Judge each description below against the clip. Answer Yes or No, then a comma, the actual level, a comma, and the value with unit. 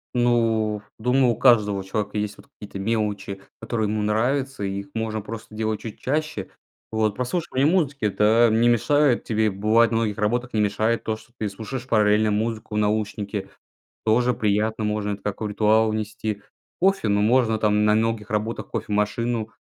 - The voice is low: Yes, low, 110 Hz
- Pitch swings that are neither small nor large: No, narrow, 1.9 semitones